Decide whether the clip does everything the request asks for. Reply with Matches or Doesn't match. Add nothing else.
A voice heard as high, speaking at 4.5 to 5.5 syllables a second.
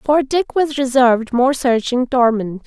Doesn't match